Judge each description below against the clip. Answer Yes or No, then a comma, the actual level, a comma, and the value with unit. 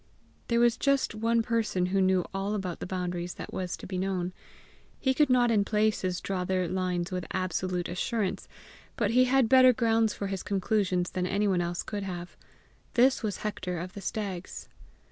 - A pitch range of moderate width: Yes, average, 3.7 semitones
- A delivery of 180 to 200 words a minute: Yes, average, 185 wpm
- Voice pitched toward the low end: No, high, 195 Hz